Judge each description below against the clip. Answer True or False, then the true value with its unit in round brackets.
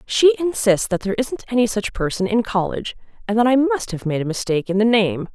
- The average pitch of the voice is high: True (215 Hz)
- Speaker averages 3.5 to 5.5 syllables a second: False (6.1 syllables/s)